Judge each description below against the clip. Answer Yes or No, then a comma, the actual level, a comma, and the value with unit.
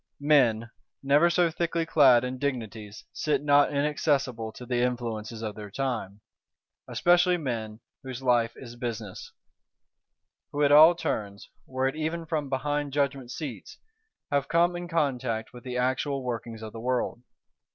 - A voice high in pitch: No, low, 130 Hz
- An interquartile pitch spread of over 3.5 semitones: Yes, average, 4.1 semitones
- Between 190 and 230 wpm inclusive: No, average, 150 wpm